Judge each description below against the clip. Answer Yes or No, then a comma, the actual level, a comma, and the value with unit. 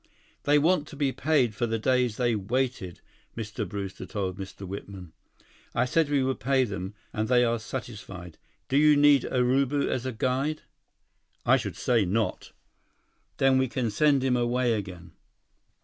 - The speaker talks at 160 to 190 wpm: Yes, average, 165 wpm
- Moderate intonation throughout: Yes, average, 4.3 semitones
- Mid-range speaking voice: No, low, 125 Hz